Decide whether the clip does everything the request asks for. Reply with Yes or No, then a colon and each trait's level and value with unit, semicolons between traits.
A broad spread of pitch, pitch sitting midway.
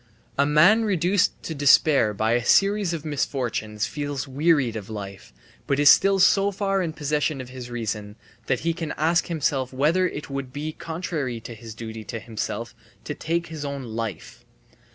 Yes: wide, 5.8 semitones; medium, 145 Hz